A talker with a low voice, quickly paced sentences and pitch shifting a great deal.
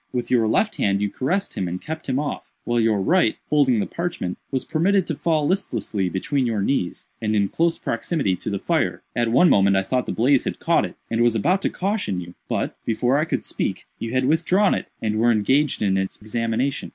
Yes: low, 120 Hz; fast, 225 wpm; wide, 6.8 semitones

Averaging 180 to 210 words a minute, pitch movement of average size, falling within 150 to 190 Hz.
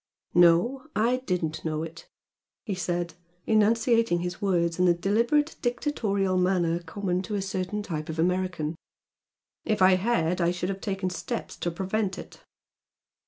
No: average, 150 wpm; average, 3.4 semitones; medium, 185 Hz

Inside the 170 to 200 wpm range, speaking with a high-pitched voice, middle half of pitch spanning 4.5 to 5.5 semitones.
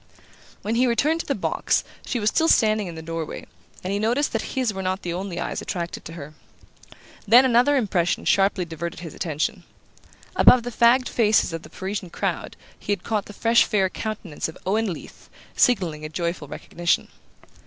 Yes: average, 185 wpm; high, 200 Hz; average, 5.1 semitones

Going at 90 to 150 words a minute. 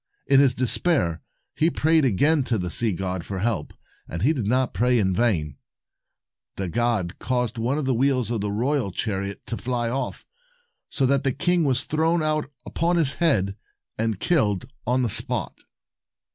No: average, 175 wpm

